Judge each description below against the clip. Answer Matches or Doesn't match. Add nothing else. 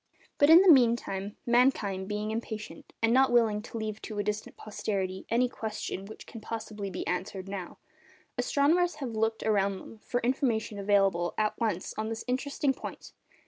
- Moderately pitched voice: Doesn't match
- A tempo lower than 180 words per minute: Matches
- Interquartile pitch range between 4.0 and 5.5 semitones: Doesn't match